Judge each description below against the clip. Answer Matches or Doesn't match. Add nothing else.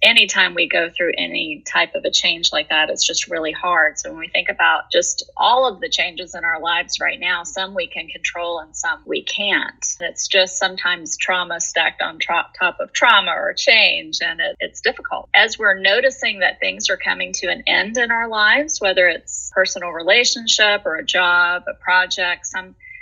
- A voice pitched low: Doesn't match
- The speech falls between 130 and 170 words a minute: Doesn't match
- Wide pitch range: Matches